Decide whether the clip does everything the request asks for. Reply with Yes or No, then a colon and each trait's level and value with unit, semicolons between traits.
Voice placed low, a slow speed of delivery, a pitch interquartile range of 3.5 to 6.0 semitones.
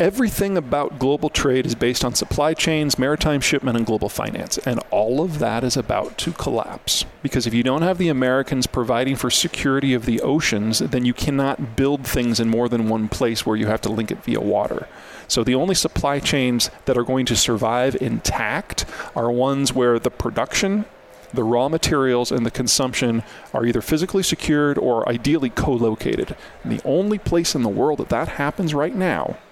No: low, 130 Hz; average, 190 wpm; average, 3.8 semitones